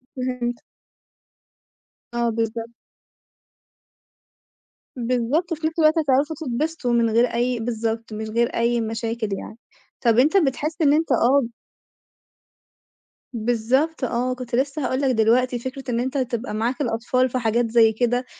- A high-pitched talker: Yes, high, 245 Hz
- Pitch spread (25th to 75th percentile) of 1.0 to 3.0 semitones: Yes, narrow, 2.6 semitones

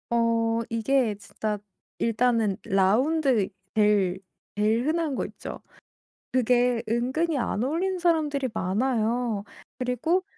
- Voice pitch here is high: Yes, high, 240 Hz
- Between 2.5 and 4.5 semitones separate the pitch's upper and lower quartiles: Yes, average, 4.1 semitones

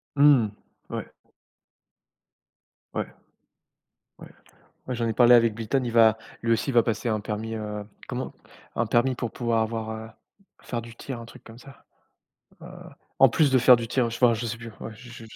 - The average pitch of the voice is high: No, low, 115 Hz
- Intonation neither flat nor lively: No, narrow, 1.5 semitones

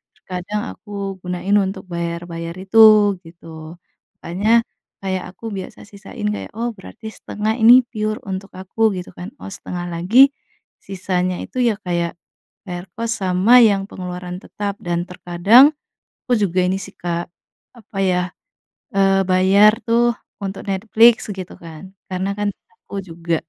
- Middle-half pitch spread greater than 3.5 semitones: No, average, 2.9 semitones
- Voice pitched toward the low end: No, high, 190 Hz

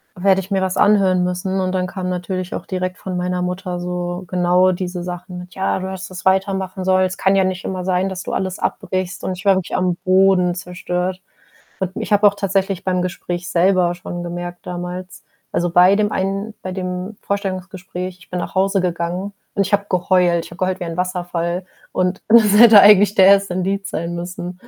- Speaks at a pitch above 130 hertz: Yes, medium, 185 Hz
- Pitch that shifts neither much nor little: No, narrow, 1.2 semitones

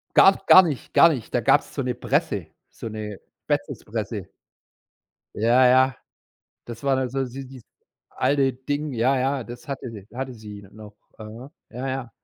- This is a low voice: Yes, low, 130 Hz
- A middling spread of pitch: Yes, average, 3.0 semitones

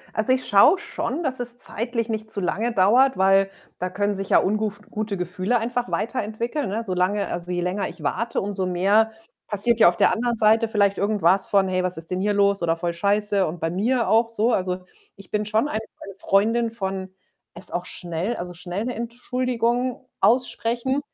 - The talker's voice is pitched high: Yes, high, 210 Hz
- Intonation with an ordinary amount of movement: Yes, average, 3.8 semitones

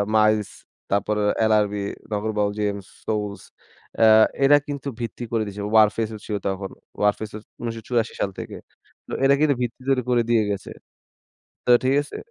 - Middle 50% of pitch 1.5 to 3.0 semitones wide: Yes, narrow, 2.5 semitones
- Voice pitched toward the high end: No, low, 110 Hz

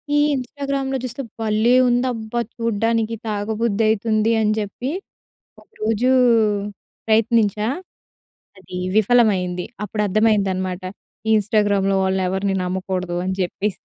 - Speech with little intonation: No, average, 3.0 semitones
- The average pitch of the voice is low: No, high, 215 Hz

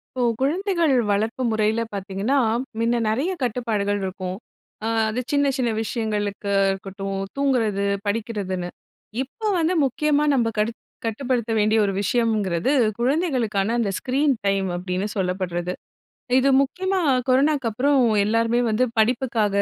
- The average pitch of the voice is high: Yes, high, 225 Hz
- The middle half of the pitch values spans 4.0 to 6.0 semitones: Yes, average, 4.7 semitones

